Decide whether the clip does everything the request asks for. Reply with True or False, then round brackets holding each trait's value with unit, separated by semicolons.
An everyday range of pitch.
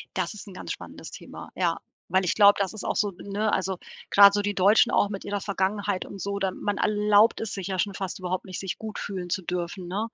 False (1.6 semitones)